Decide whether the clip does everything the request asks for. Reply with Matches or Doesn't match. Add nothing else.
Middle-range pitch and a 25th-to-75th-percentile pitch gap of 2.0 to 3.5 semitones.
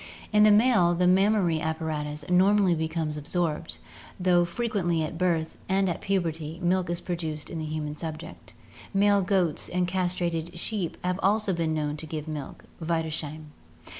Matches